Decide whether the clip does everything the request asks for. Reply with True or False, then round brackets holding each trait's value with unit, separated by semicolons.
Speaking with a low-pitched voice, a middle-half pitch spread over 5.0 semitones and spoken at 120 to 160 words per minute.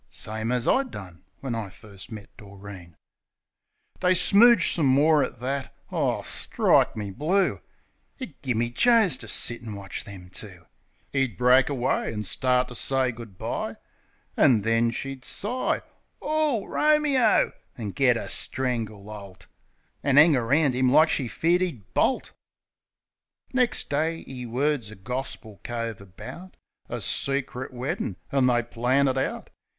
True (125 Hz; 5.6 semitones; 155 wpm)